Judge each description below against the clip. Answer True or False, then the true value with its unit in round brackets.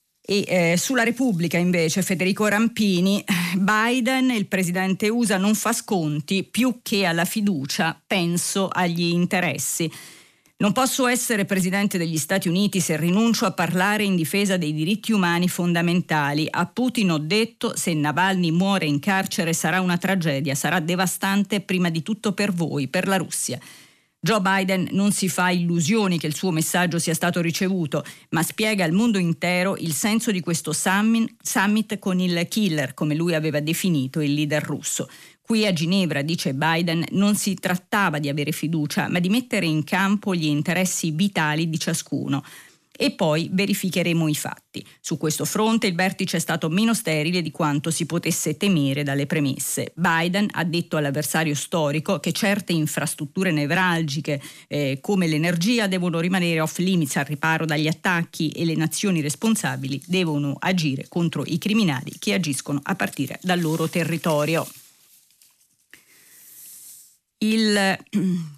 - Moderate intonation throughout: True (3.7 semitones)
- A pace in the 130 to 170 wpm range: True (150 wpm)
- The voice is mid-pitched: True (175 Hz)